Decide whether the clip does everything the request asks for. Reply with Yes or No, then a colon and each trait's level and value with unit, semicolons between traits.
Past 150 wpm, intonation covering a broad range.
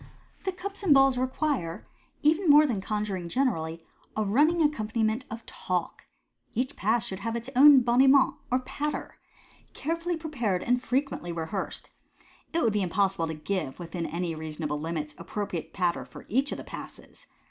Yes: average, 170 wpm; wide, 7.9 semitones